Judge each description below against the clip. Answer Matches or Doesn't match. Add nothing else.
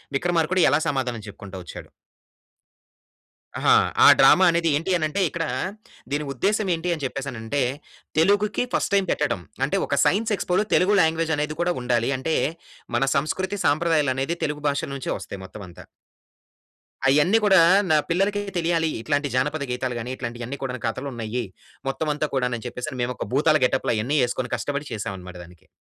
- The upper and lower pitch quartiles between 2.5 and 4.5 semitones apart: Doesn't match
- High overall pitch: Doesn't match